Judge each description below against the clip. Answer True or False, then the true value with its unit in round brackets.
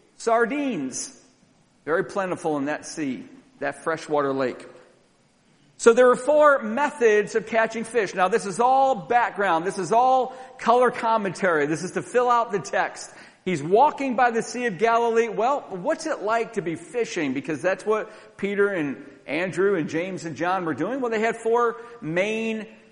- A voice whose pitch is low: False (225 Hz)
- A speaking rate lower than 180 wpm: True (170 wpm)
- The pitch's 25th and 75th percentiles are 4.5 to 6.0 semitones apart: True (4.8 semitones)